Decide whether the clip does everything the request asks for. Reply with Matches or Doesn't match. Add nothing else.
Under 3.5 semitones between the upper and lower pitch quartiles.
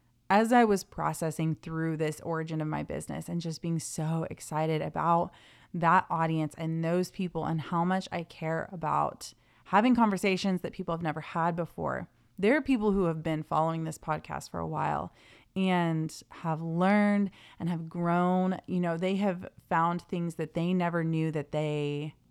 Matches